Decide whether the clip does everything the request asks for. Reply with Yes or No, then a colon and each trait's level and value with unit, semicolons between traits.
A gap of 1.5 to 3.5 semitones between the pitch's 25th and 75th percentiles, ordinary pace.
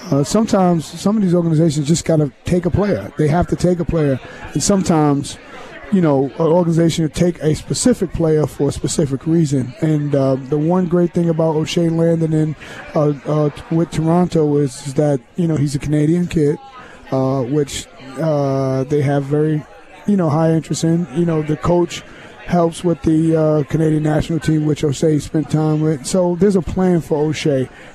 Yes: narrow, 2.4 semitones; average, 190 wpm